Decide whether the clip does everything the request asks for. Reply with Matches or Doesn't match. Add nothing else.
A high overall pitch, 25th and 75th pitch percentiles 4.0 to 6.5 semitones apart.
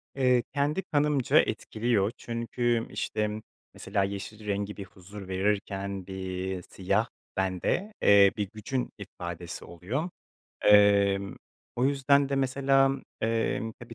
Doesn't match